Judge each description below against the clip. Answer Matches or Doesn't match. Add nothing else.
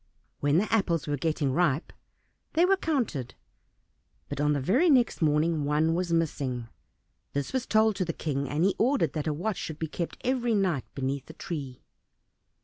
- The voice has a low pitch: Doesn't match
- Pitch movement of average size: Doesn't match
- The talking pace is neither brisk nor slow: Matches